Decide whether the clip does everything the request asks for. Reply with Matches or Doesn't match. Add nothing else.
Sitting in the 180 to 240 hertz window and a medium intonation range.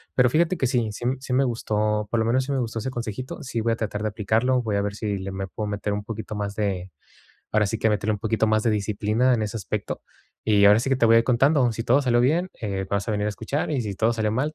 Doesn't match